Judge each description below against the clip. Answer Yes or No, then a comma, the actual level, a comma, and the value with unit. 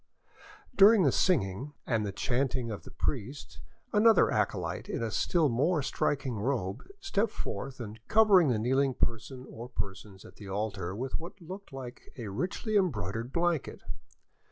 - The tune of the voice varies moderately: No, wide, 7.9 semitones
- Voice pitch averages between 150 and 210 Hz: No, low, 130 Hz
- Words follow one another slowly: No, average, 155 wpm